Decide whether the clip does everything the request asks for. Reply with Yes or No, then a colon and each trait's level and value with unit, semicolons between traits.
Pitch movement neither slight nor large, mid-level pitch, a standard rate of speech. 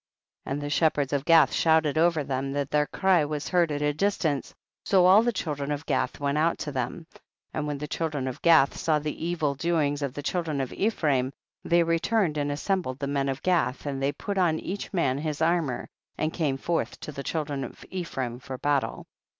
No: average, 3.1 semitones; medium, 150 Hz; fast, 220 wpm